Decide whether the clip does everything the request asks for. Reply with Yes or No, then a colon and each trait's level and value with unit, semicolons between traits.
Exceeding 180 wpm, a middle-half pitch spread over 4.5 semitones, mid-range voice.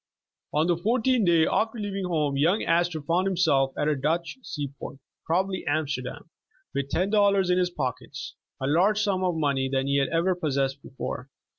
Yes: average, 190 wpm; average, 5.1 semitones; medium, 165 Hz